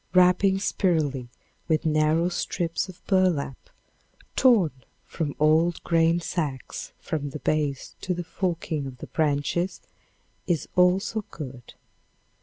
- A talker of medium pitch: Yes, medium, 165 Hz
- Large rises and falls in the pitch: No, average, 3.3 semitones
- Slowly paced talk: Yes, slow, 115 wpm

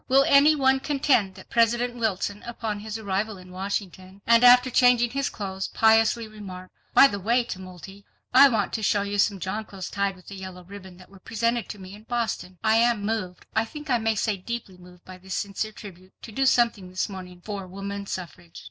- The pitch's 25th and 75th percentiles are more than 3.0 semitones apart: Yes, average, 3.7 semitones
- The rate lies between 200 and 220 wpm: Yes, fast, 205 wpm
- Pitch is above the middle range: Yes, high, 205 Hz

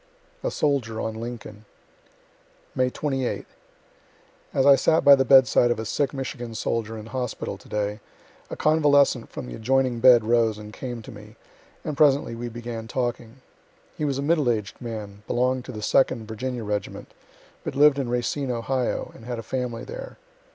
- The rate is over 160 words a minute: Yes, average, 170 wpm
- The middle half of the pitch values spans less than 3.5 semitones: Yes, average, 3.1 semitones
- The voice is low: Yes, low, 120 Hz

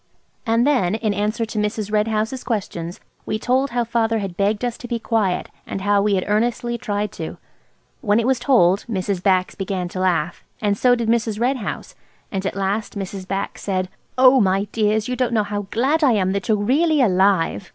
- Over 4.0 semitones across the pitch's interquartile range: No, average, 3.3 semitones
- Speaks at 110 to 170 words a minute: No, fast, 205 wpm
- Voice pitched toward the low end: No, high, 210 Hz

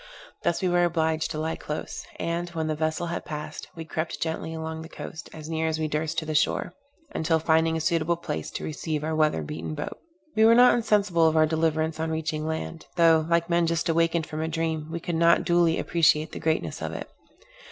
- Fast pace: Yes, fast, 220 wpm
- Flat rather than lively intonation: Yes, narrow, 1.1 semitones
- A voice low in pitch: No, medium, 160 Hz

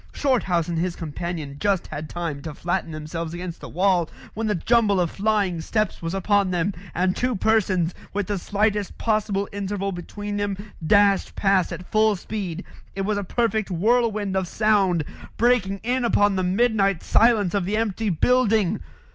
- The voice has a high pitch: Yes, high, 195 Hz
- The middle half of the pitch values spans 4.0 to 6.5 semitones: No, average, 3.4 semitones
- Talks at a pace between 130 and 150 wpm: No, average, 170 wpm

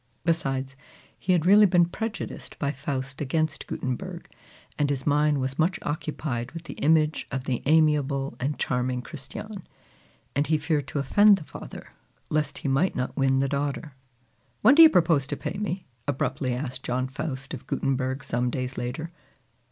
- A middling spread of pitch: Yes, average, 3.4 semitones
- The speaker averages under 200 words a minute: Yes, average, 165 wpm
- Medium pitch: Yes, medium, 145 Hz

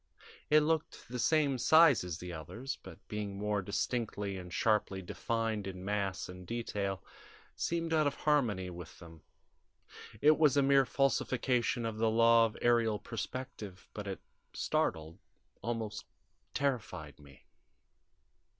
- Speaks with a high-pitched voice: No, low, 110 Hz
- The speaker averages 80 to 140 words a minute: Yes, slow, 135 wpm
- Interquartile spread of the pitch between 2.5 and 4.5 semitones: No, average, 5.3 semitones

